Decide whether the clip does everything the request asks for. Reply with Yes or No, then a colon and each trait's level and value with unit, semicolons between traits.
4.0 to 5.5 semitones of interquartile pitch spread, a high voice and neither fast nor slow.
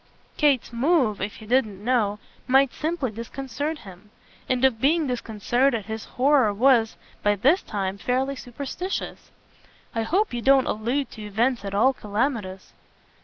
Yes: average, 4.3 semitones; high, 245 Hz; average, 145 wpm